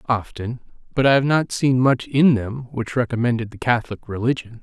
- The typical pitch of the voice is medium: No, low, 120 Hz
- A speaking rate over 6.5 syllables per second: No, 5.4 syllables/s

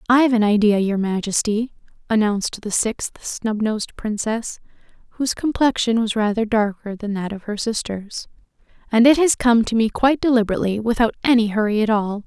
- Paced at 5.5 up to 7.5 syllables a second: Yes, 5.6 syllables/s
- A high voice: Yes, high, 220 Hz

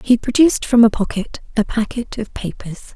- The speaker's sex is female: Yes, female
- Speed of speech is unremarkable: Yes, average, 185 wpm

